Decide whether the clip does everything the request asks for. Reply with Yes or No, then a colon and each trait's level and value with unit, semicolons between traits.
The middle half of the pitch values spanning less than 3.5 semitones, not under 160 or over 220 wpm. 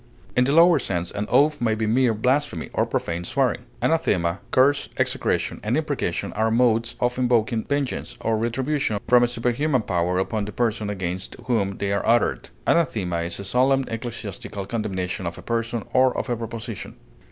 No: average, 4.2 semitones; average, 175 wpm